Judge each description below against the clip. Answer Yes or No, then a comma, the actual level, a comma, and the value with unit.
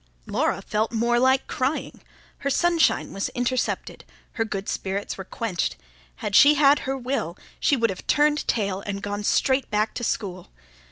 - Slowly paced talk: No, average, 165 wpm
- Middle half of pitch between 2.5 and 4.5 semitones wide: No, average, 5.1 semitones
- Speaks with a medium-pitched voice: No, high, 230 Hz